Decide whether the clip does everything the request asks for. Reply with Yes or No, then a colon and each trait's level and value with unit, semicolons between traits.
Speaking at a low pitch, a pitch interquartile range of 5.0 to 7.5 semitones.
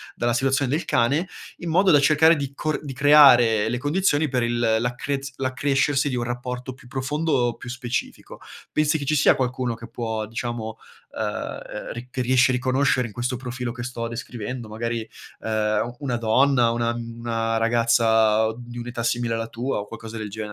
No: low, 120 Hz; average, 2.7 semitones